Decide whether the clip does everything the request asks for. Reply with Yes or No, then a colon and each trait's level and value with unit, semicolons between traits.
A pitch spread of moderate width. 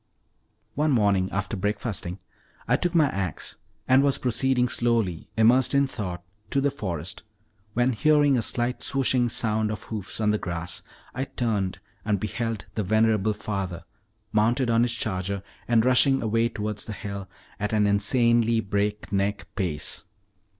Yes: average, 3.5 semitones